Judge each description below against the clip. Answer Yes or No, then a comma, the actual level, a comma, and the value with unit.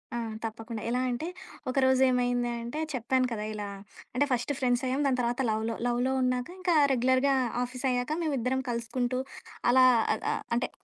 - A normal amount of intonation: No, narrow, 1.5 semitones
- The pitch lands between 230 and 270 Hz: Yes, very high, 250 Hz